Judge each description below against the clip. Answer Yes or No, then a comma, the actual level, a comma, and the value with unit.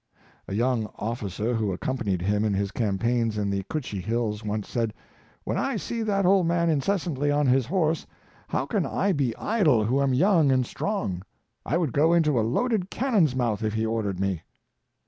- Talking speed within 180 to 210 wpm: Yes, average, 190 wpm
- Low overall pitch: Yes, low, 125 Hz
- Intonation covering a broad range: Yes, wide, 7.6 semitones